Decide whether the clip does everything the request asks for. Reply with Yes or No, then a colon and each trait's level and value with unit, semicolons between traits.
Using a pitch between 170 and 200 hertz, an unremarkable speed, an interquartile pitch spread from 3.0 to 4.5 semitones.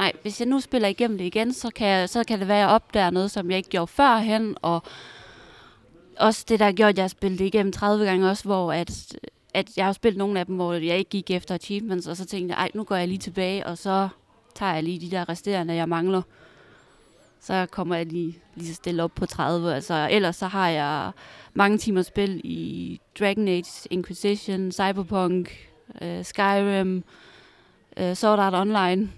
No: high, 190 Hz; average, 205 wpm; narrow, 2.4 semitones